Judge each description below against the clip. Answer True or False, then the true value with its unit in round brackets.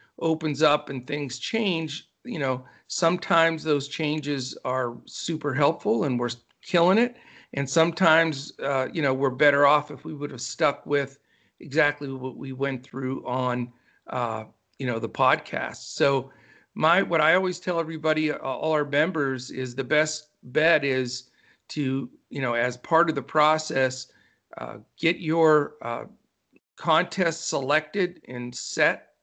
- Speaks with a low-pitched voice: False (145 Hz)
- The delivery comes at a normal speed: True (150 wpm)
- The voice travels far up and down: False (3.4 semitones)